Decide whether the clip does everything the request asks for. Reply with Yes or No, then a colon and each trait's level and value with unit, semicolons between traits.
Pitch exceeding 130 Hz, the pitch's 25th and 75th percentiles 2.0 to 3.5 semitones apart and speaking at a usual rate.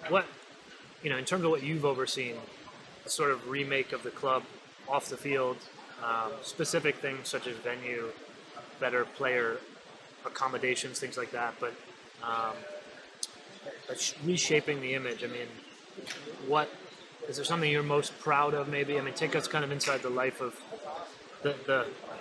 Yes: medium, 140 Hz; average, 2.8 semitones; average, 160 wpm